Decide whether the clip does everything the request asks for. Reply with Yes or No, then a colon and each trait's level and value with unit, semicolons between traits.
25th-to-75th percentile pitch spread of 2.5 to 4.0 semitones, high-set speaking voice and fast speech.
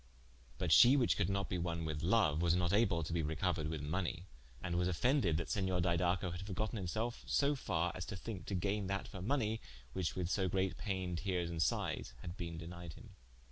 No: average, 2.8 semitones; very low, 90 Hz; fast, 215 wpm